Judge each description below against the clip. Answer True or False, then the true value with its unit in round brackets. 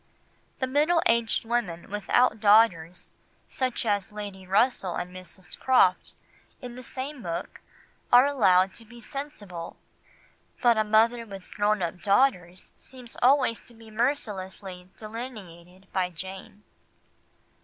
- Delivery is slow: True (125 wpm)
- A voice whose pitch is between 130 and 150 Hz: False (215 Hz)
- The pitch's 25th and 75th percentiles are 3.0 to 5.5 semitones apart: True (4.6 semitones)